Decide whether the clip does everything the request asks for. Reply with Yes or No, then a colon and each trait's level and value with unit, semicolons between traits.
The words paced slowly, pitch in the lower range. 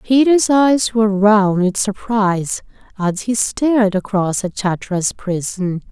No: slow, 130 wpm; high, 210 Hz